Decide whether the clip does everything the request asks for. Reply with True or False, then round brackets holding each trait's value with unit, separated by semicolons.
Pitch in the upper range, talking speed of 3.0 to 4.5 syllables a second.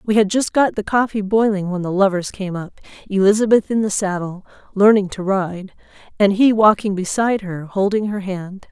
False (200 Hz; 5.2 syllables/s)